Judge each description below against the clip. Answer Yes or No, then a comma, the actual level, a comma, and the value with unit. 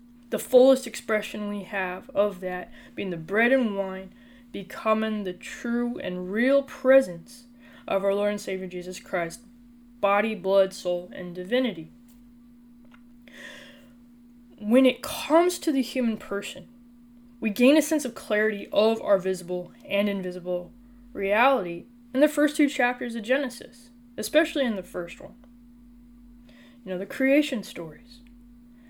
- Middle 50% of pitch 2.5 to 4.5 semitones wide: Yes, average, 3.7 semitones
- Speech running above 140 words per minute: No, slow, 135 wpm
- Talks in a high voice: Yes, high, 240 Hz